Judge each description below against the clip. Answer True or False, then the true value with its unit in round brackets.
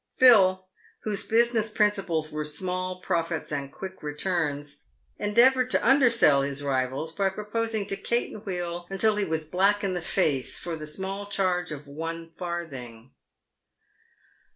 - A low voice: False (180 Hz)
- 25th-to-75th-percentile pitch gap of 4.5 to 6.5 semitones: True (5.2 semitones)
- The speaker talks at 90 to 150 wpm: True (140 wpm)